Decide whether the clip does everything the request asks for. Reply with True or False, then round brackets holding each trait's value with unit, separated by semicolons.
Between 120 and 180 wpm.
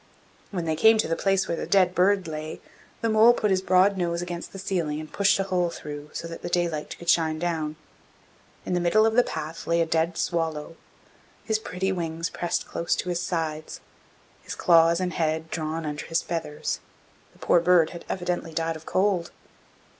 False (200 wpm)